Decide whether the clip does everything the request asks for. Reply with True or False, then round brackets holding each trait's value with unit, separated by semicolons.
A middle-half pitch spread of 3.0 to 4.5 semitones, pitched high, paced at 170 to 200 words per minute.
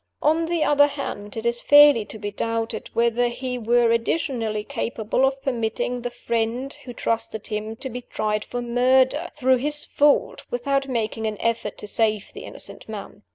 True (3.3 semitones; 240 Hz; 175 wpm)